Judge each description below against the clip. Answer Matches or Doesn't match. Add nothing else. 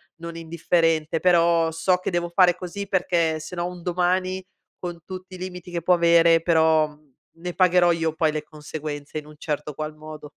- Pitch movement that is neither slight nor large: Doesn't match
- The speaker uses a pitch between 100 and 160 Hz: Doesn't match